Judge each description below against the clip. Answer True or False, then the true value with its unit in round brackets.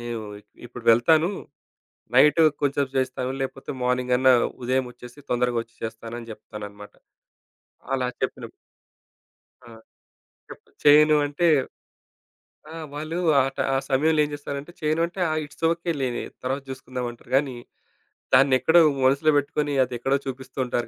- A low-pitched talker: True (130 Hz)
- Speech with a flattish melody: False (3.1 semitones)